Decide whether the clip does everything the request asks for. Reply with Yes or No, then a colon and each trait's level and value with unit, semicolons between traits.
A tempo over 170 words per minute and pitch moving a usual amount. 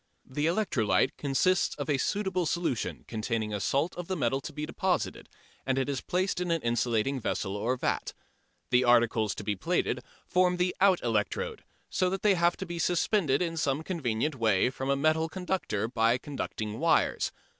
No: average, 180 wpm; wide, 7.1 semitones